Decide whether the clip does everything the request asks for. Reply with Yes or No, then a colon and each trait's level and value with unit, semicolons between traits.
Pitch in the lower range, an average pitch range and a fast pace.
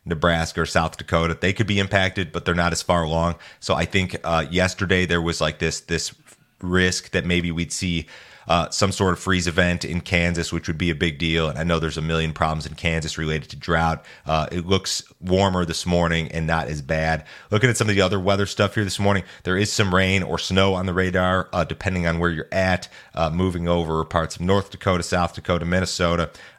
No: very low, 85 Hz; narrow, 2.3 semitones; fast, 230 wpm